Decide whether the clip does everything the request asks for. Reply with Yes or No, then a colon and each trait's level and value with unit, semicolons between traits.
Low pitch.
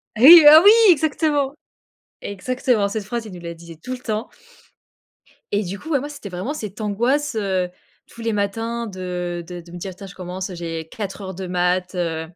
No: high, 200 Hz